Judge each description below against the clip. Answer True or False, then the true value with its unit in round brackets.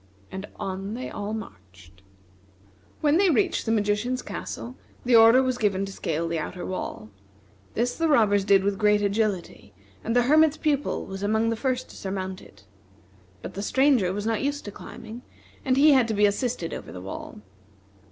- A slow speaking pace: False (180 wpm)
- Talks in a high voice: True (210 Hz)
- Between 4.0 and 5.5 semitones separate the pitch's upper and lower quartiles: True (4.6 semitones)